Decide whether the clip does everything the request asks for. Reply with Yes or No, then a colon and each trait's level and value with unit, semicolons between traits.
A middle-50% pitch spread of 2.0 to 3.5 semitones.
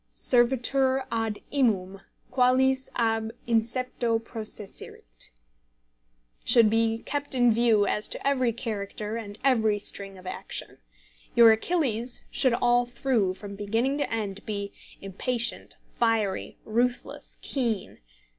Yes: average, 3.1 semitones